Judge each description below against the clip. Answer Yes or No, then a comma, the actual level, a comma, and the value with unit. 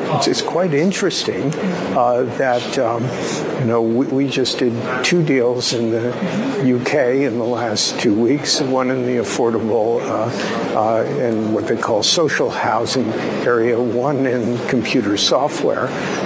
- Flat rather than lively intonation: Yes, narrow, 1.9 semitones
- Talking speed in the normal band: Yes, average, 145 wpm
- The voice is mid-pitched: No, low, 125 Hz